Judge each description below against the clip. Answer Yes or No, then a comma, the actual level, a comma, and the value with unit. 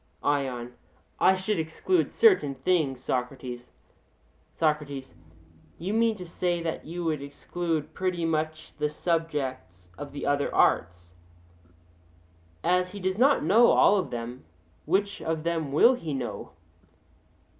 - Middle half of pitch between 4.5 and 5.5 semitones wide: Yes, average, 4.9 semitones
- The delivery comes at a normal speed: No, slow, 130 wpm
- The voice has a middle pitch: Yes, medium, 160 Hz